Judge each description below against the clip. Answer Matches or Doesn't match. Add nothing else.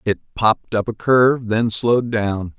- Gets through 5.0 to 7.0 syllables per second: Doesn't match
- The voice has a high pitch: Doesn't match